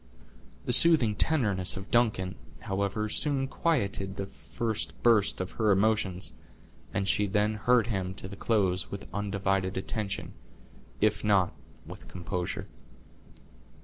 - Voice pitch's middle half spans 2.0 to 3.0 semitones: Yes, narrow, 2.6 semitones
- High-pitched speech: No, low, 100 Hz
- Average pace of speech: No, slow, 125 wpm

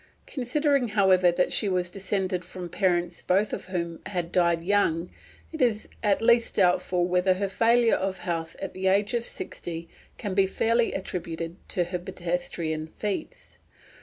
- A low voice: No, medium, 185 Hz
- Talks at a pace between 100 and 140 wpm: No, average, 160 wpm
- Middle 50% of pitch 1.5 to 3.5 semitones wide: Yes, average, 2.9 semitones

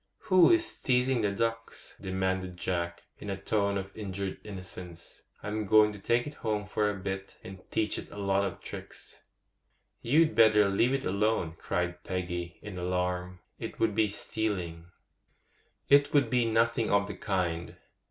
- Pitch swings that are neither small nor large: Yes, average, 3.3 semitones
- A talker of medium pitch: No, low, 100 Hz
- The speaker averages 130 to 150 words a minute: No, average, 160 wpm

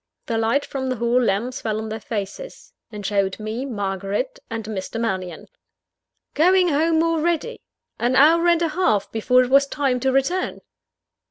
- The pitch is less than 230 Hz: No, very high, 250 Hz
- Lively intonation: Yes, wide, 6.4 semitones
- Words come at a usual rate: Yes, average, 165 wpm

